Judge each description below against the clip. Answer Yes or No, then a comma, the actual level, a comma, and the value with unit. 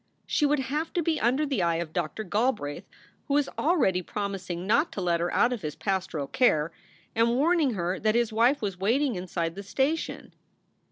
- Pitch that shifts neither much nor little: No, wide, 7.3 semitones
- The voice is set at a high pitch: Yes, high, 215 Hz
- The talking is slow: No, average, 190 wpm